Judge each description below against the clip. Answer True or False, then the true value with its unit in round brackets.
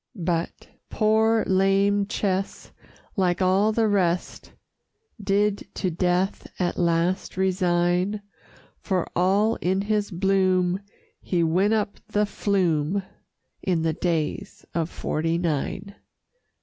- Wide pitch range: False (2.5 semitones)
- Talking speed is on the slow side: True (110 wpm)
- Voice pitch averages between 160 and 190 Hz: True (185 Hz)